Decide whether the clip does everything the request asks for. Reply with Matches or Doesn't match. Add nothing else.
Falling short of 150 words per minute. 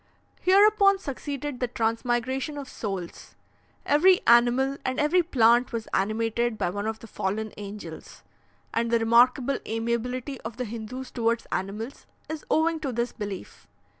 Matches